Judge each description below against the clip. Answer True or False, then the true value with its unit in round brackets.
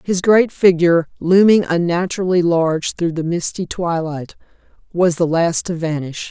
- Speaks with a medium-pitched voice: True (170 Hz)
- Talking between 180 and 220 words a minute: False (145 wpm)